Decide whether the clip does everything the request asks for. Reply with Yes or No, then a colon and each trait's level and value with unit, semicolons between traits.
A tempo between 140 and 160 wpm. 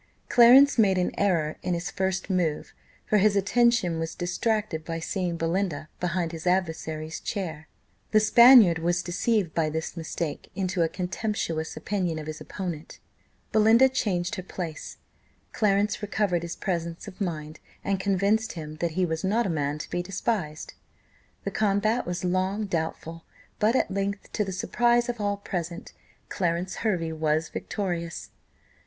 Yes: average, 155 wpm